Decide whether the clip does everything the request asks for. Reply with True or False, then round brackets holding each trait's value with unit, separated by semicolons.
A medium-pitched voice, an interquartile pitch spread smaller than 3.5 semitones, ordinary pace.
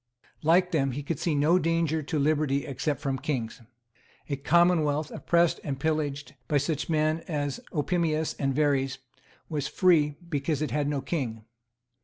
True (150 Hz; 2.4 semitones; 155 wpm)